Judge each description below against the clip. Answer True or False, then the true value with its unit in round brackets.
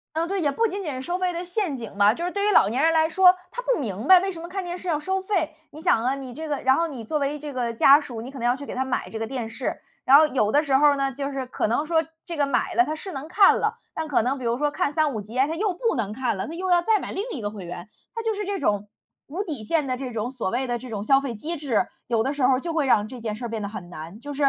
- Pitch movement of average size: False (5.9 semitones)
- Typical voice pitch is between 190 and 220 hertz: False (280 Hz)